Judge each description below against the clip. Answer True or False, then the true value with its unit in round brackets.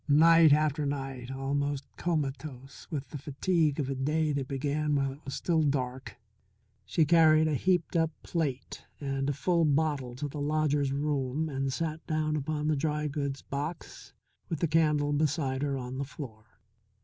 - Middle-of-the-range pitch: True (145 Hz)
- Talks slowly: False (170 wpm)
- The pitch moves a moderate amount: False (2.3 semitones)